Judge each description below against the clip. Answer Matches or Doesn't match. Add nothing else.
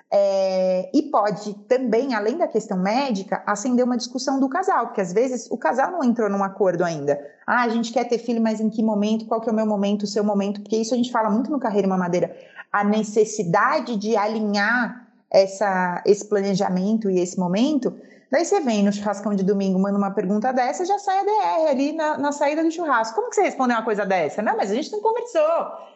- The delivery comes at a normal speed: Doesn't match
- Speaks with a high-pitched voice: Matches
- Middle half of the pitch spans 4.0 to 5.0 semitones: Matches